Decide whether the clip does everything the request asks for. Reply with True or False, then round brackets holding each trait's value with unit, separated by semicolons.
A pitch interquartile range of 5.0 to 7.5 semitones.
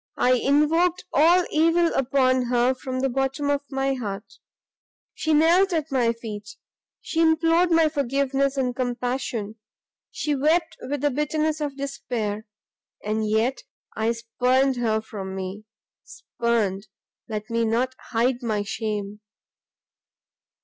False (4.6 semitones)